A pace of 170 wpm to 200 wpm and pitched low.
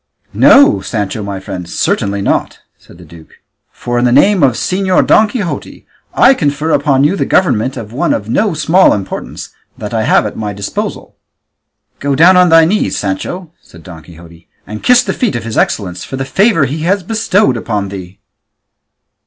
Yes: average, 185 wpm; low, 130 Hz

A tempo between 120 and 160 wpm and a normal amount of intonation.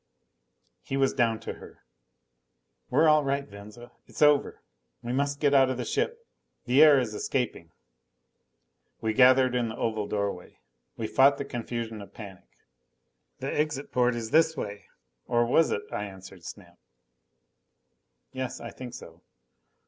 Yes: average, 150 wpm; average, 4.4 semitones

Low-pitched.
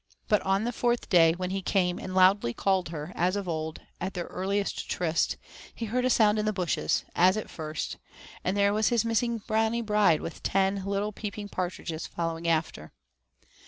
No: high, 195 Hz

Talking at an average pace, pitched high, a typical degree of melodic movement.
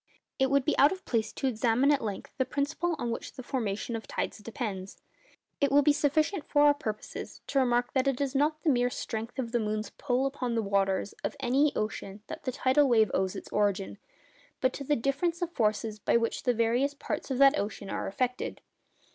No: fast, 220 wpm; very high, 250 Hz; average, 4.3 semitones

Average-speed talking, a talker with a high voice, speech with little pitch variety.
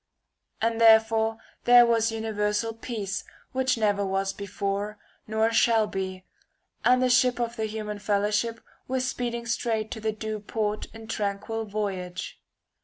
Yes: average, 150 wpm; high, 220 Hz; narrow, 1.8 semitones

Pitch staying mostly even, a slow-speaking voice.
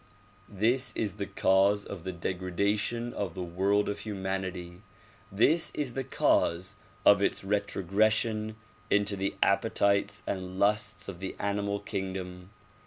Yes: narrow, 1.7 semitones; slow, 130 wpm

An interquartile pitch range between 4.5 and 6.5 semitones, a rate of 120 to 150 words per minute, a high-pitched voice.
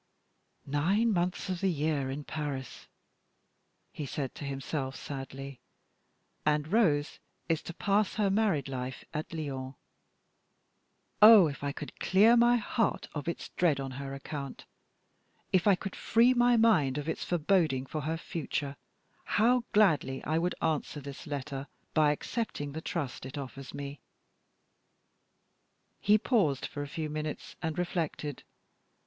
No: average, 5.2 semitones; average, 140 wpm; medium, 155 Hz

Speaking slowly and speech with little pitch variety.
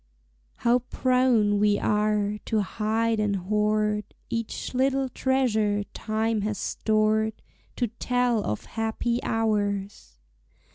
Yes: slow, 105 wpm; narrow, 2.0 semitones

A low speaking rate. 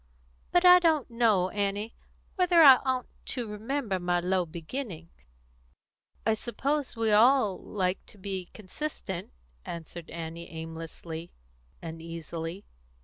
Yes: slow, 115 wpm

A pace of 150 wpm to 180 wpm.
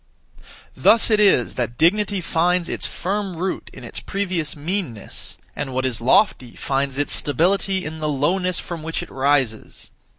Yes: average, 160 wpm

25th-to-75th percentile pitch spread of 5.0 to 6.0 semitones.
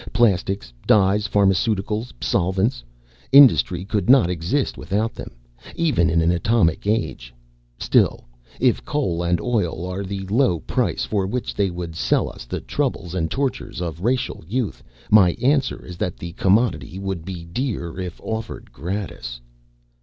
No: average, 4.6 semitones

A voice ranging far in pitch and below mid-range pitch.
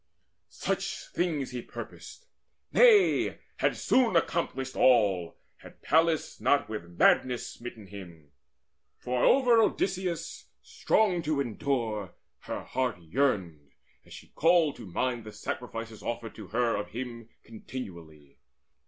Yes: wide, 7.0 semitones; low, 120 Hz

